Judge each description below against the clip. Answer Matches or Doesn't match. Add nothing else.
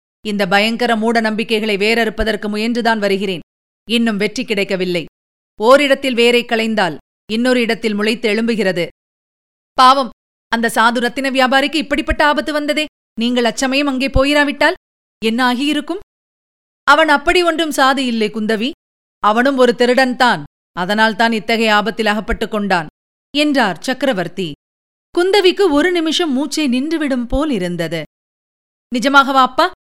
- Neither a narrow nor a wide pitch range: Matches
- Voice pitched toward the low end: Doesn't match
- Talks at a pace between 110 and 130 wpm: Matches